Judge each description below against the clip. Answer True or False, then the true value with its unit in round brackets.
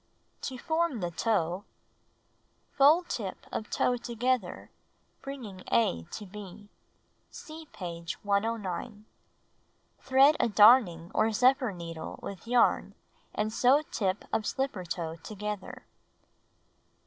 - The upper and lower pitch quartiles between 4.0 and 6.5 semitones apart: True (5.5 semitones)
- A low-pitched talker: False (215 Hz)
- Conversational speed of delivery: False (110 wpm)